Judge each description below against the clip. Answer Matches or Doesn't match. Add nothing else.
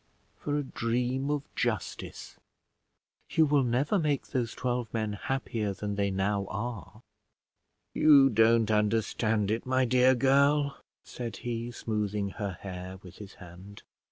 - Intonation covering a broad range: Doesn't match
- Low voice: Matches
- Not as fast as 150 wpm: Matches